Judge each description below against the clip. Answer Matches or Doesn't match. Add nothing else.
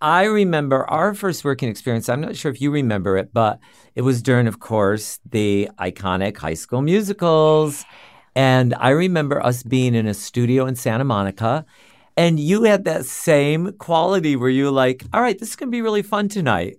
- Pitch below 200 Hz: Matches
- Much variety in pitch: Matches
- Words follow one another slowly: Doesn't match